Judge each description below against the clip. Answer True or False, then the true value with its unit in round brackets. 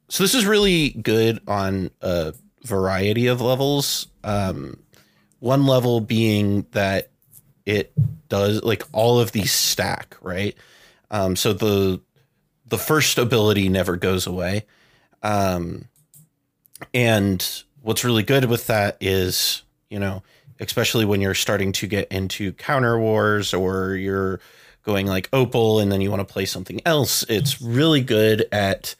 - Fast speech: False (140 wpm)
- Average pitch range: True (4.0 semitones)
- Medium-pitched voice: False (105 Hz)